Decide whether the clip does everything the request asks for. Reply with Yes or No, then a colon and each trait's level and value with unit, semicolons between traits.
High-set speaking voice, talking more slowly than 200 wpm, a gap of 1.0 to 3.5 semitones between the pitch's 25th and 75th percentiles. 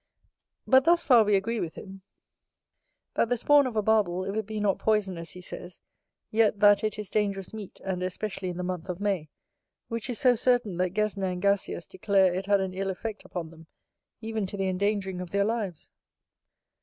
No: high, 200 Hz; fast, 205 wpm; average, 2.8 semitones